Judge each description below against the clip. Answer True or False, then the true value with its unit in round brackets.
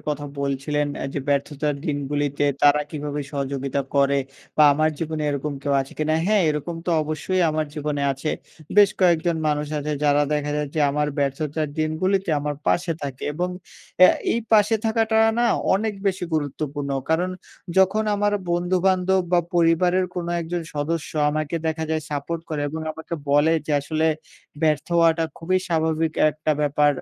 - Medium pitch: True (155 Hz)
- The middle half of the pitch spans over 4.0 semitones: False (3.0 semitones)